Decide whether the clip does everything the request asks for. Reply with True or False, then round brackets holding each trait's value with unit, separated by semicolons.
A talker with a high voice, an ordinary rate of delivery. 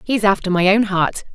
False (195 Hz; 225 wpm)